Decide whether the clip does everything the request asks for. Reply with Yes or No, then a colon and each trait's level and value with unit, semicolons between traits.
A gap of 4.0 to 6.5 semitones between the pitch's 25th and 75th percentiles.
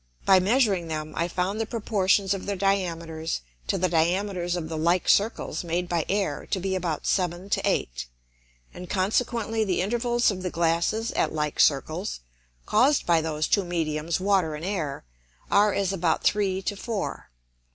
No: average, 3.5 semitones